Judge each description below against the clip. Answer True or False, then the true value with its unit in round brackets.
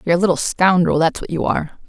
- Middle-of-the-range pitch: True (175 Hz)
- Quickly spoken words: True (255 wpm)